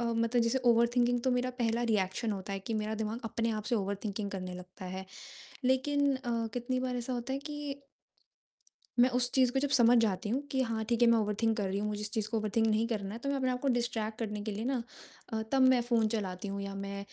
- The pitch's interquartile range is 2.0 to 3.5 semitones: Yes, average, 2.9 semitones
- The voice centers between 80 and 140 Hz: No, high, 230 Hz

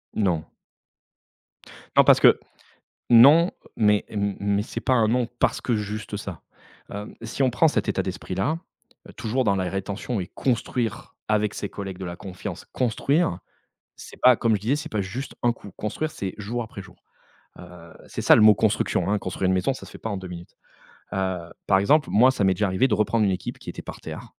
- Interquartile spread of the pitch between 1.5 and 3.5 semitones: No, average, 3.9 semitones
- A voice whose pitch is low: Yes, low, 105 Hz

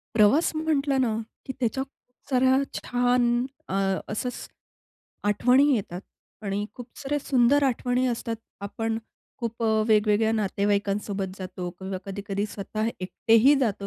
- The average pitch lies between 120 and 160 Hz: No, high, 225 Hz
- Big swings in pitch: No, average, 4.0 semitones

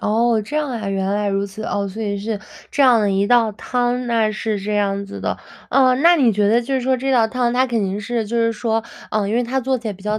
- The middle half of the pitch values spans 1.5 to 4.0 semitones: Yes, average, 3.1 semitones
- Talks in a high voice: Yes, high, 225 Hz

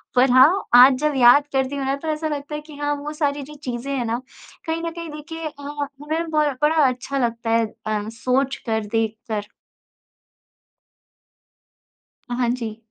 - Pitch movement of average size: Yes, average, 3.9 semitones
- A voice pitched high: Yes, very high, 275 Hz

